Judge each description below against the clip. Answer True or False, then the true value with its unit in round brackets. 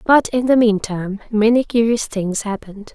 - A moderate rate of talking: True (165 wpm)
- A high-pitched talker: True (220 Hz)